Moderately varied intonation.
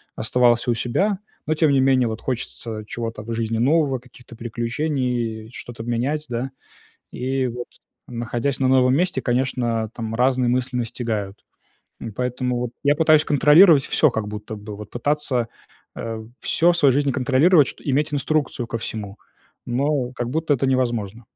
Yes: average, 3.3 semitones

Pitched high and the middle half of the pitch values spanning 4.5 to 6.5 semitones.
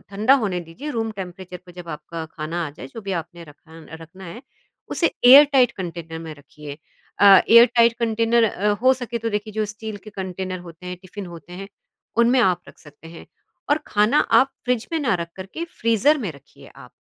Yes: high, 195 Hz; wide, 5.4 semitones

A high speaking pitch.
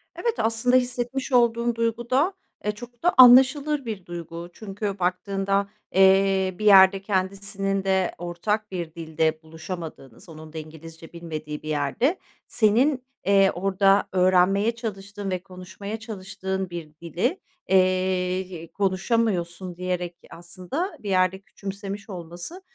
Yes: high, 195 Hz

